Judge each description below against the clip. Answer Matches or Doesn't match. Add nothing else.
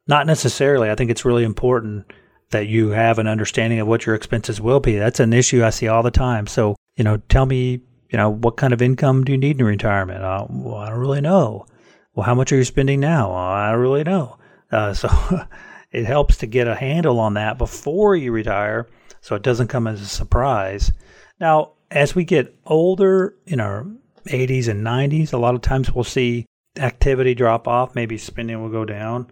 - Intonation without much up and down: Doesn't match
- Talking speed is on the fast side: Matches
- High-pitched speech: Doesn't match